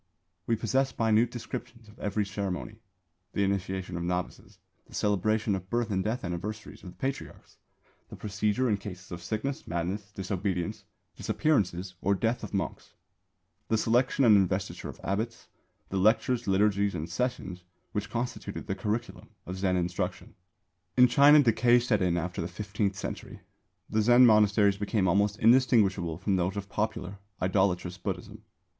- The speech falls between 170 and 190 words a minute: No, average, 150 wpm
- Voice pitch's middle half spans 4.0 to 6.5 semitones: No, average, 3.2 semitones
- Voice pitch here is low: Yes, low, 100 Hz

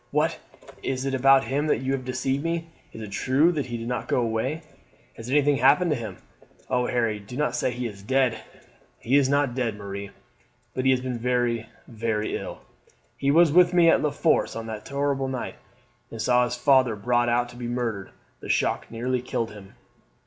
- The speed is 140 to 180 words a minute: No, average, 200 wpm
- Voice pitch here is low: Yes, low, 125 Hz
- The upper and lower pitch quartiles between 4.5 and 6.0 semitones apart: No, average, 3.0 semitones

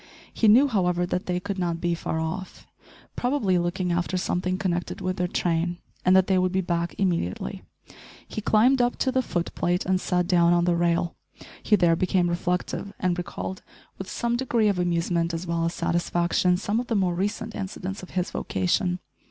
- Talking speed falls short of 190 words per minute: No, average, 195 wpm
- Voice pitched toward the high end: No, medium, 180 Hz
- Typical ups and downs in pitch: No, narrow, 2.0 semitones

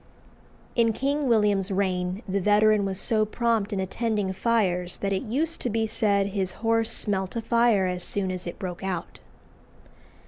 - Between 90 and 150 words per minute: No, average, 170 wpm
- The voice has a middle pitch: No, high, 205 Hz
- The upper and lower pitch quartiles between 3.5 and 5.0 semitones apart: No, average, 3.1 semitones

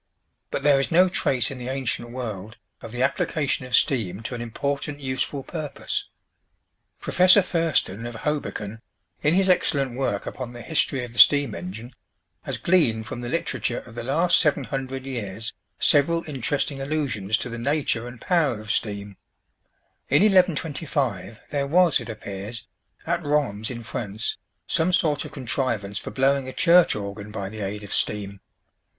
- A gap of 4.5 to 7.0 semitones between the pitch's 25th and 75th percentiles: Yes, average, 4.9 semitones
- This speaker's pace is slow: No, average, 165 wpm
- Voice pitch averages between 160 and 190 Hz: No, low, 130 Hz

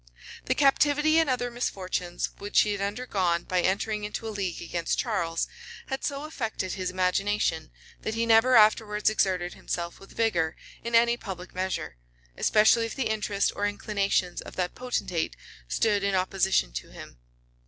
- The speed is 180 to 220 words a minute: No, average, 165 wpm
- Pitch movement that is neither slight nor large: Yes, average, 4.0 semitones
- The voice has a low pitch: No, high, 205 Hz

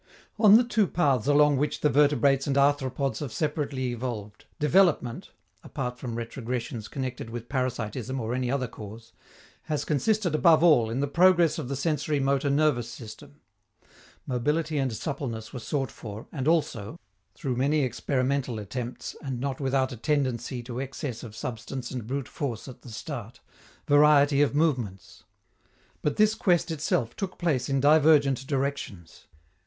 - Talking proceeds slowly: No, average, 155 wpm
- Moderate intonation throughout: Yes, average, 3.6 semitones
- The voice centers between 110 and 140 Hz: Yes, low, 135 Hz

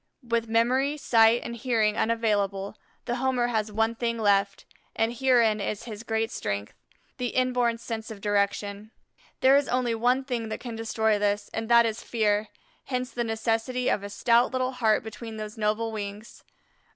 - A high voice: Yes, high, 225 Hz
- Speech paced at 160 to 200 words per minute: Yes, average, 170 wpm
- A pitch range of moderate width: No, narrow, 2.2 semitones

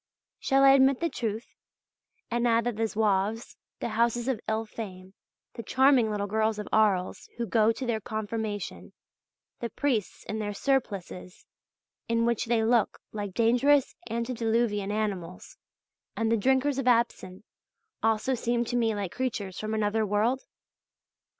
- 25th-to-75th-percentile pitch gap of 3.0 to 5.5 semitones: No, narrow, 2.5 semitones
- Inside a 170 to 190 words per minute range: No, average, 150 wpm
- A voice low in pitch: No, high, 225 Hz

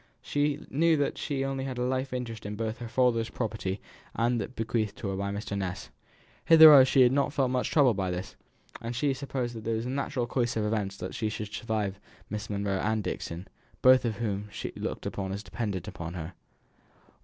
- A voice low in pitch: Yes, low, 115 Hz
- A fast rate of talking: Yes, fast, 210 wpm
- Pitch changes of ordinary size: Yes, average, 4.2 semitones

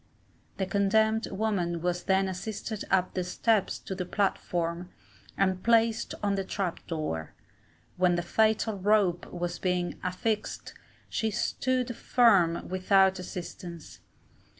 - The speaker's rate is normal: No, slow, 125 wpm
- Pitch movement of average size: Yes, average, 3.5 semitones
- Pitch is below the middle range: No, high, 190 Hz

